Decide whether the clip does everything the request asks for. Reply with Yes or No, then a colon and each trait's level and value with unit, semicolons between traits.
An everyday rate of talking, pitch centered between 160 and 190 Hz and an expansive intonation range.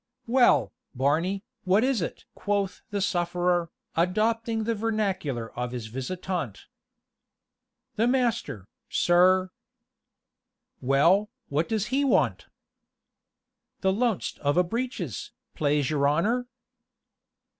No: slow, 105 wpm; medium, 185 Hz; wide, 6.6 semitones